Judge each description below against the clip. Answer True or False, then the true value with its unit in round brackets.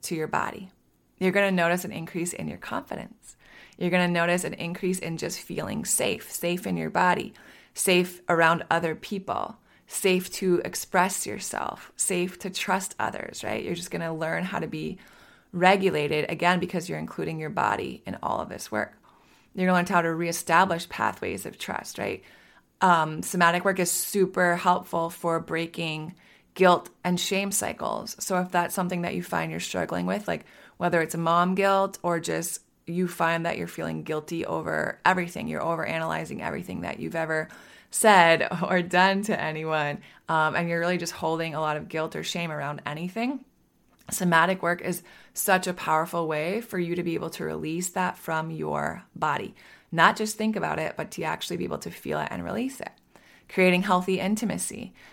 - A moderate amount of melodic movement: False (2.3 semitones)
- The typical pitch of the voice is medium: True (175 Hz)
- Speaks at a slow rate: False (185 wpm)